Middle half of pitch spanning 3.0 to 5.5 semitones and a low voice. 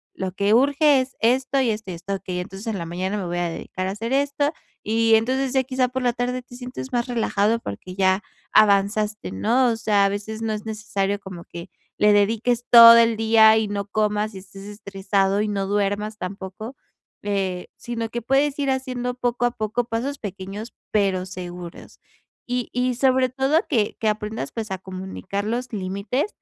No: average, 3.9 semitones; high, 215 Hz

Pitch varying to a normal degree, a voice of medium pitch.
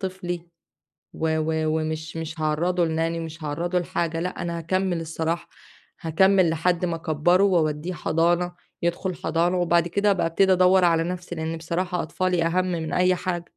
No: narrow, 1.9 semitones; medium, 170 Hz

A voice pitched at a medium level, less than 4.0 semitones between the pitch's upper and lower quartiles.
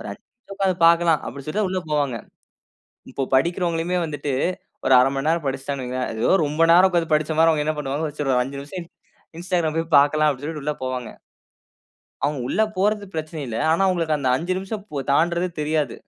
Yes: medium, 155 Hz; average, 3.5 semitones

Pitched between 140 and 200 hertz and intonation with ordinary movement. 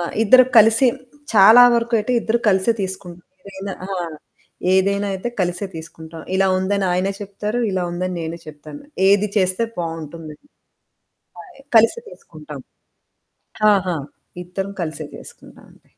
Yes: high, 190 Hz; average, 3.3 semitones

